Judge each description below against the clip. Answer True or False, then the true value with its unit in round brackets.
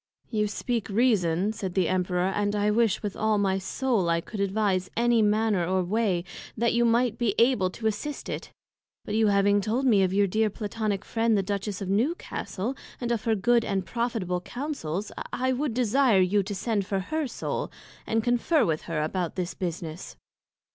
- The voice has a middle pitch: False (210 Hz)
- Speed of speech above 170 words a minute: True (190 wpm)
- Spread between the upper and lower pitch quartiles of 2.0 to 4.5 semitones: True (3.7 semitones)